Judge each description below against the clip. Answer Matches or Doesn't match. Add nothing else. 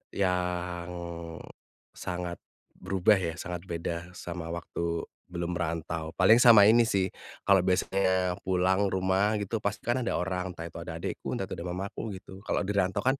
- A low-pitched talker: Matches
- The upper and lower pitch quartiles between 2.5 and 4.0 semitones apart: Doesn't match